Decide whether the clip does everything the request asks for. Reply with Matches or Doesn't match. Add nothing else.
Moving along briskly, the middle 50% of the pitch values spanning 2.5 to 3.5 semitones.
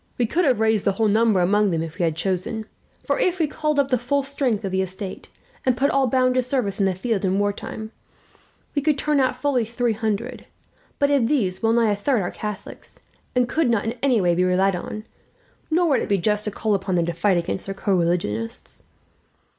Doesn't match